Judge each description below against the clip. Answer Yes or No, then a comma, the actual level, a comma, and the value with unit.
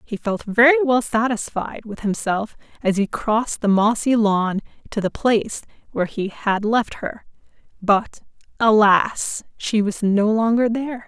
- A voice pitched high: Yes, high, 220 Hz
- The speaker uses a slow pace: No, average, 150 wpm